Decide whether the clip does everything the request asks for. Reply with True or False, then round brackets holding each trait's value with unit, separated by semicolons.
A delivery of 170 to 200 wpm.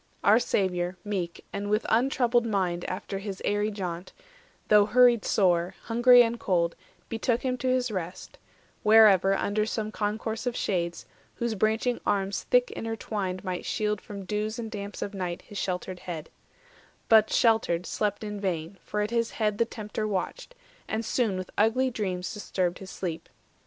False (160 wpm)